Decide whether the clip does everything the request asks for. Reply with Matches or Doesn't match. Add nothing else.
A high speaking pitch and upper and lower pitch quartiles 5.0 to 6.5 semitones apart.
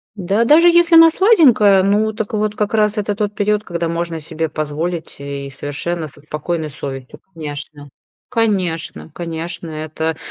Doesn't match